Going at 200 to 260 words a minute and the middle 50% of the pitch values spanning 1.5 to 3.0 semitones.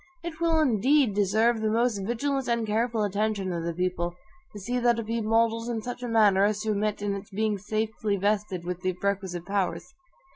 Yes: fast, 205 wpm; average, 2.7 semitones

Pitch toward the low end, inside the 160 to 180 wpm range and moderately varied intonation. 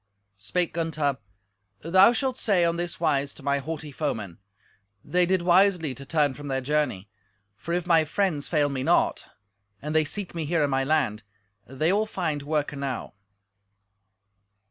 No: medium, 155 Hz; average, 165 wpm; average, 3.7 semitones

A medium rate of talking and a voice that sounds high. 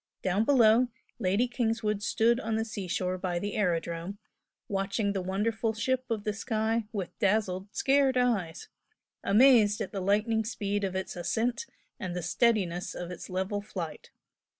Yes: average, 150 wpm; high, 205 Hz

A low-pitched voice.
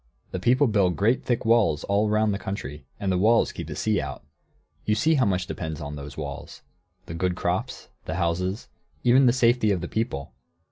Yes: low, 100 Hz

